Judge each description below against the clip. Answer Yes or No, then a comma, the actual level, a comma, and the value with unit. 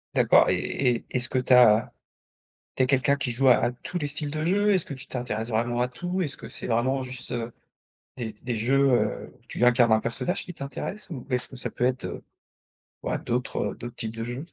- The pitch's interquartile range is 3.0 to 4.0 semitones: No, narrow, 2.5 semitones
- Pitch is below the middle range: Yes, low, 125 Hz